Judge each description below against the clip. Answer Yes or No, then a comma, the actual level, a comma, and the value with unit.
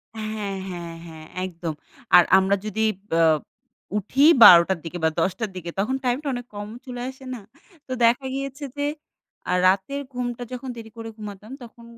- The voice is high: Yes, high, 220 Hz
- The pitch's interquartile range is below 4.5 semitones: No, average, 4.9 semitones